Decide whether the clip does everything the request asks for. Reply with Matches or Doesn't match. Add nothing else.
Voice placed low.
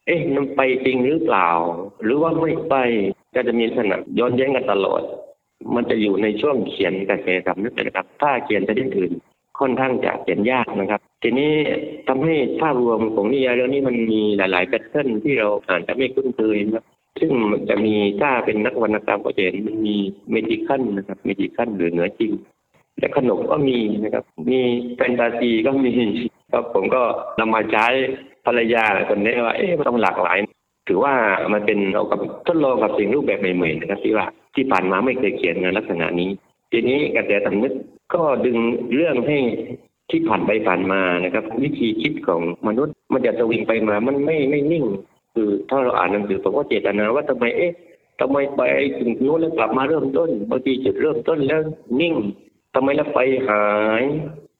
Matches